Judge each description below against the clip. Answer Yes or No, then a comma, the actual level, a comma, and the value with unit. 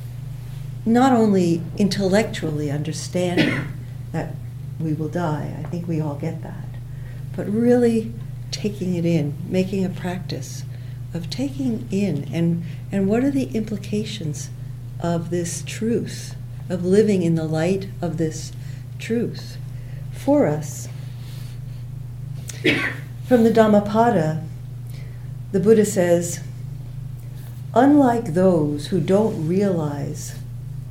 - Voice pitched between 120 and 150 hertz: Yes, medium, 140 Hz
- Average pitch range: No, wide, 5.7 semitones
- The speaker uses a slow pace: Yes, slow, 105 wpm